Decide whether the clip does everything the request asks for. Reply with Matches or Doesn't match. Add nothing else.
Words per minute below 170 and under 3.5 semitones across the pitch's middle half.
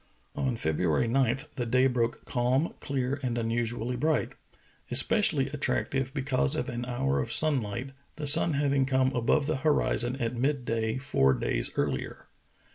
Matches